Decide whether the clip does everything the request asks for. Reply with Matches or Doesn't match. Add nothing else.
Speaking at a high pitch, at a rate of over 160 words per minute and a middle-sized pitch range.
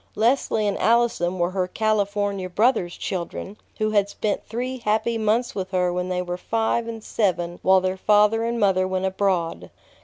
Matches